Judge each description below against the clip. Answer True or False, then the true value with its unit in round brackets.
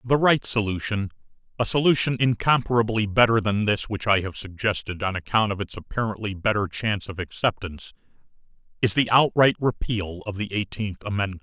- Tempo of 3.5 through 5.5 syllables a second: False (5.7 syllables/s)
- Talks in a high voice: False (105 Hz)